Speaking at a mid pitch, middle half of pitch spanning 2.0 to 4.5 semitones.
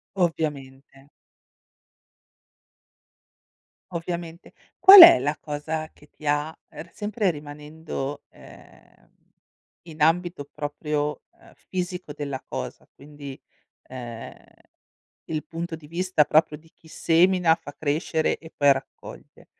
Yes: medium, 155 Hz; narrow, 2.6 semitones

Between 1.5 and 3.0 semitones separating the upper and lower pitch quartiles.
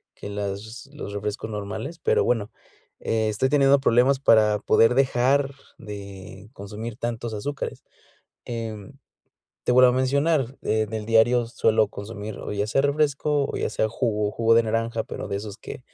No: average, 3.7 semitones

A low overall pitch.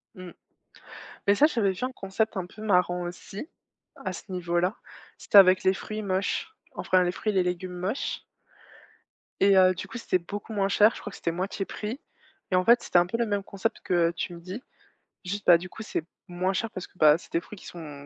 No: medium, 185 Hz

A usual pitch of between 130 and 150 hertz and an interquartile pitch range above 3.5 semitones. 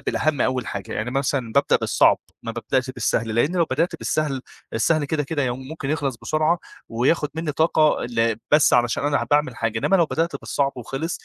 Yes: medium, 140 Hz; average, 4.5 semitones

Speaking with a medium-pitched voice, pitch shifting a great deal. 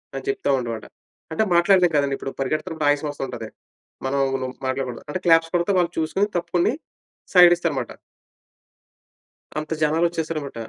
No: medium, 160 Hz; average, 3.8 semitones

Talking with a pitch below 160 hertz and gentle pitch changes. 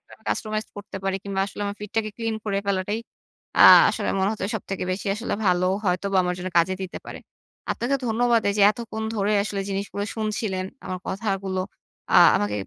No: high, 200 Hz; narrow, 2.2 semitones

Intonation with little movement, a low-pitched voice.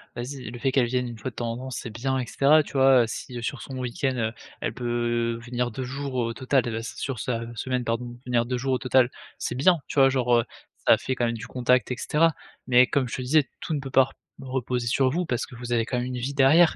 Yes: narrow, 1.9 semitones; low, 125 Hz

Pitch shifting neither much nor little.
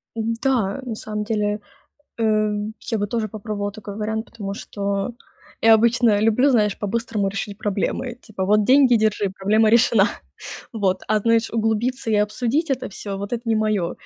No: narrow, 2.0 semitones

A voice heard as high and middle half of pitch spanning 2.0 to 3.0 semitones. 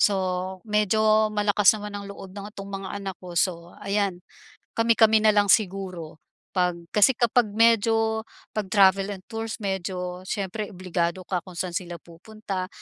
Yes: high, 200 Hz; average, 2.7 semitones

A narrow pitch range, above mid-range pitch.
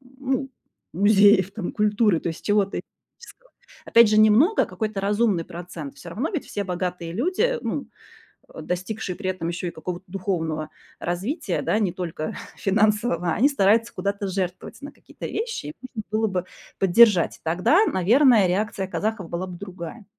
No: average, 4.0 semitones; high, 200 Hz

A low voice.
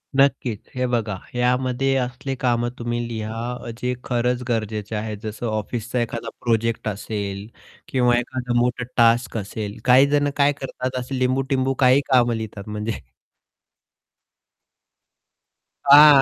Yes: low, 120 Hz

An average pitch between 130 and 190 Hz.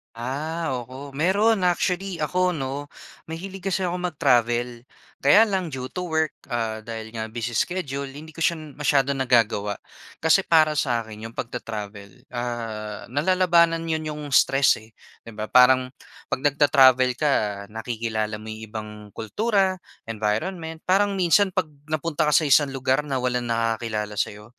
Yes: low, 135 Hz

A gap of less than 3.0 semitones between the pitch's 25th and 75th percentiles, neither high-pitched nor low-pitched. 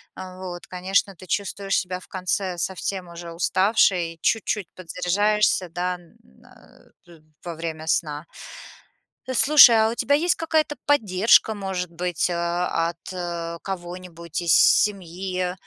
Yes: narrow, 2.5 semitones; medium, 180 Hz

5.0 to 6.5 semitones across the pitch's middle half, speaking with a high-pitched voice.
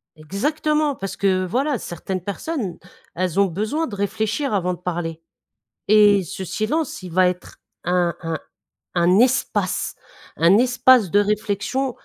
Yes: wide, 5.5 semitones; high, 200 Hz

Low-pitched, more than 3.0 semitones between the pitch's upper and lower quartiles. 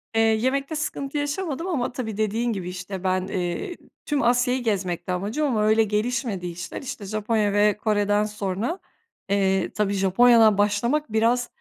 No: high, 215 Hz; average, 3.8 semitones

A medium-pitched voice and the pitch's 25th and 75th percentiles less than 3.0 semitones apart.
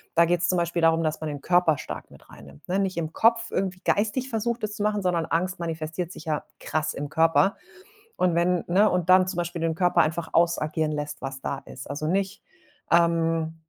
Yes: medium, 170 Hz; narrow, 2.6 semitones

